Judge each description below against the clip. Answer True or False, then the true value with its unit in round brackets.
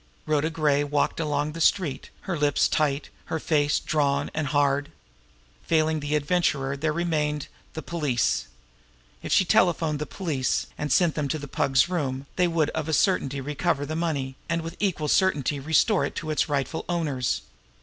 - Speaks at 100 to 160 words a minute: False (175 wpm)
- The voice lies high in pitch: False (150 Hz)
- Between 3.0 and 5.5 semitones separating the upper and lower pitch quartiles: False (2.4 semitones)